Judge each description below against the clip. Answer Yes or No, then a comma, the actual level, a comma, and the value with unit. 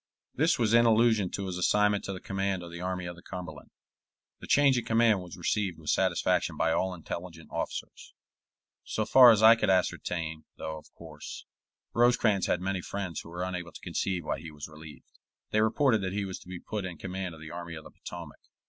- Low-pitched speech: Yes, very low, 95 Hz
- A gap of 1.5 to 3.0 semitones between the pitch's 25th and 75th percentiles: No, average, 3.8 semitones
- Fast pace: Yes, fast, 210 wpm